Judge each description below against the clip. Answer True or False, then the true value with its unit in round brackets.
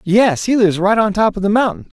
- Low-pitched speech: False (200 Hz)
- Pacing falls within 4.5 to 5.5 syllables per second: False (6.0 syllables/s)